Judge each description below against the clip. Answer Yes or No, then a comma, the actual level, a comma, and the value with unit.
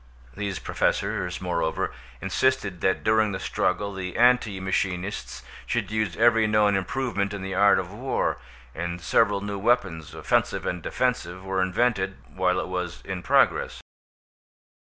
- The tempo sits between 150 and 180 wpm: No, average, 140 wpm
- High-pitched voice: No, very low, 95 Hz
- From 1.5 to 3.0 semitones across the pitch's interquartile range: Yes, average, 2.7 semitones